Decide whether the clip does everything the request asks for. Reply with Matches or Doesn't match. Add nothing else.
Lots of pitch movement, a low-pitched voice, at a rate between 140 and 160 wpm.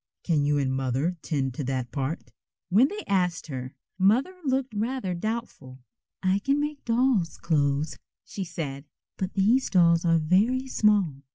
Doesn't match